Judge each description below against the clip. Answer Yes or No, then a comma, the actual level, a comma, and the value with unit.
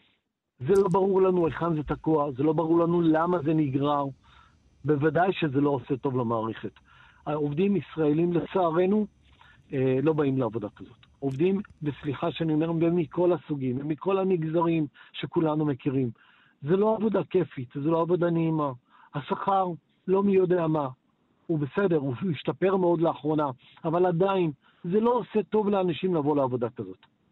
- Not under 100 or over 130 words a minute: No, average, 145 wpm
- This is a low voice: No, medium, 160 Hz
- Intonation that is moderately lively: Yes, average, 3.9 semitones